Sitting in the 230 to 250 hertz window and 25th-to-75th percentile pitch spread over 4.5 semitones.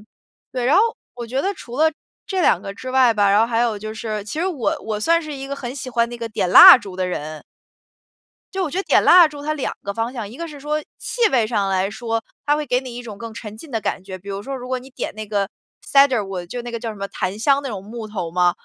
Yes: high, 235 Hz; average, 5.0 semitones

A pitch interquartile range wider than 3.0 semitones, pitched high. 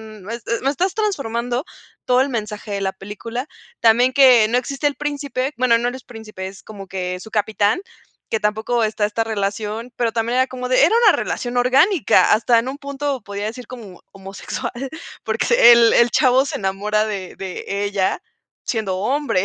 Yes: average, 3.6 semitones; high, 230 Hz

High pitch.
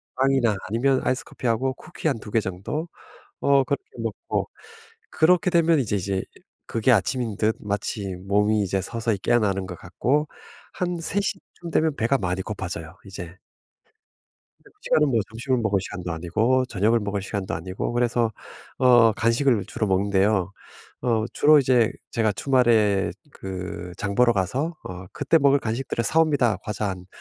No: low, 110 Hz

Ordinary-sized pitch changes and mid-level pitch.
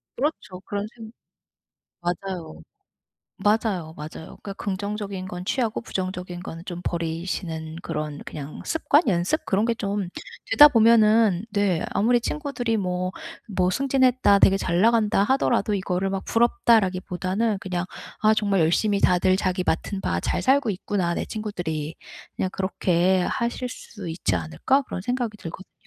No: average, 3.9 semitones; high, 195 Hz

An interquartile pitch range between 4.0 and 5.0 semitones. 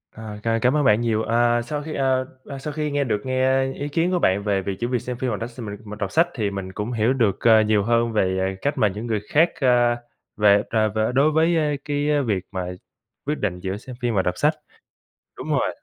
Yes: average, 4.7 semitones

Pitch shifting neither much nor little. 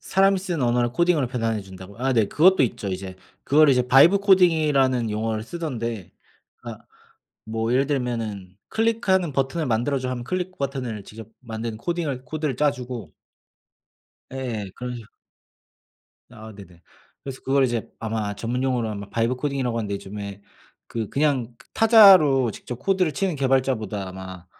Yes: average, 5.0 semitones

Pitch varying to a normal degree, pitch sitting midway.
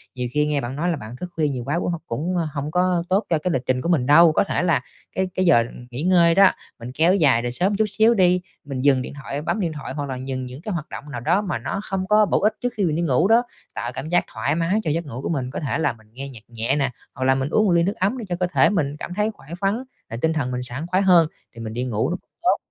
No: wide, 5.8 semitones; medium, 155 Hz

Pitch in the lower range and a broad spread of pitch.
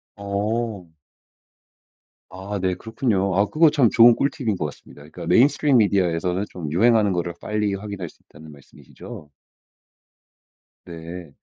No: low, 100 Hz; average, 4.2 semitones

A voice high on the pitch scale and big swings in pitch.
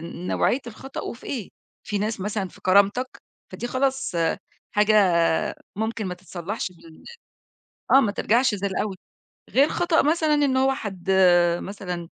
Yes: high, 210 Hz; wide, 5.7 semitones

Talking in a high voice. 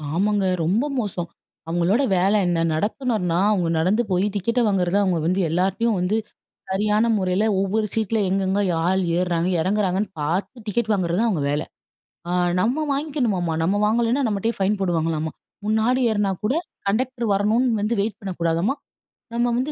Yes: high, 200 Hz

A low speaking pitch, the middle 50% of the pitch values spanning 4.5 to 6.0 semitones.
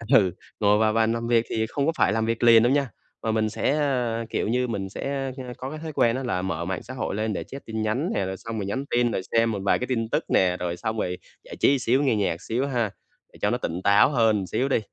No: low, 115 Hz; average, 3.7 semitones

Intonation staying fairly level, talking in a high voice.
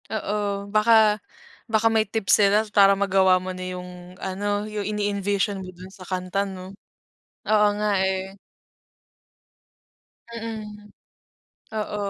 Yes: narrow, 2.0 semitones; high, 200 Hz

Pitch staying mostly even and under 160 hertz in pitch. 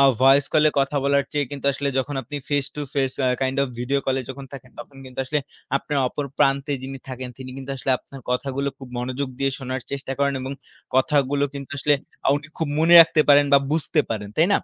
Yes: narrow, 1.5 semitones; medium, 140 Hz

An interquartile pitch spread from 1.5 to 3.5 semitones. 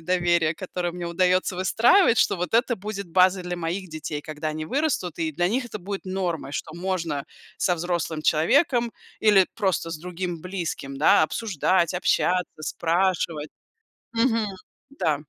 Yes: average, 2.9 semitones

